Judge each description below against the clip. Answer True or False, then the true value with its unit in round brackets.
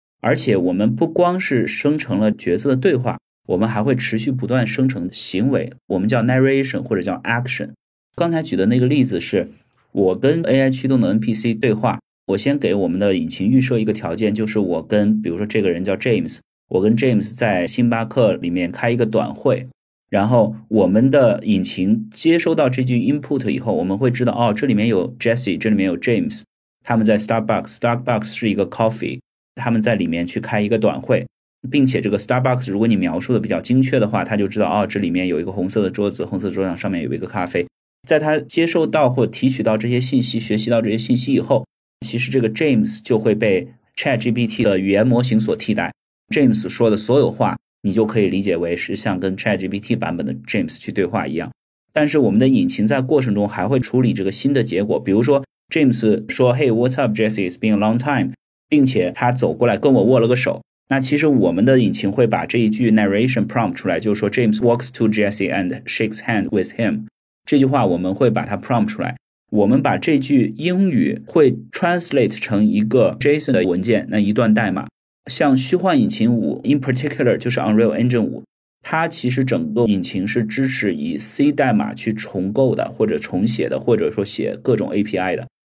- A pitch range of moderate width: True (3.9 semitones)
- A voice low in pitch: True (115 Hz)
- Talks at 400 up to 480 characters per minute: True (425 characters per minute)